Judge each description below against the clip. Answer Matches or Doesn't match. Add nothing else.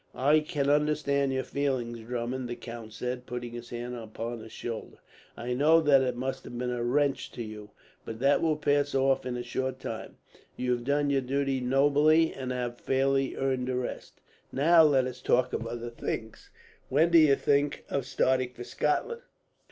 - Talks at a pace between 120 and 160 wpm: Doesn't match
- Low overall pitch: Matches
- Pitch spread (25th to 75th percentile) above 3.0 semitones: Doesn't match